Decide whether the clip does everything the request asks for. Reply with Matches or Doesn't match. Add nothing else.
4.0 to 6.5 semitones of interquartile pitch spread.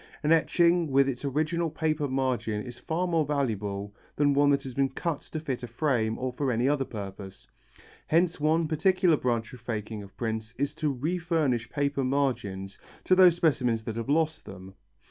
Matches